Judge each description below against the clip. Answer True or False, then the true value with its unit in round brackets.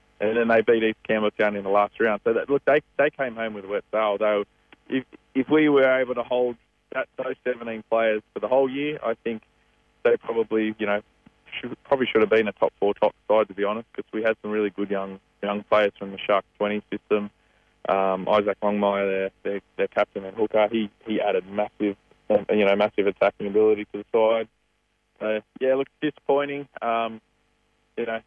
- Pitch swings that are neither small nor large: False (2.2 semitones)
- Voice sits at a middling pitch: False (110 Hz)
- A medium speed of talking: False (210 wpm)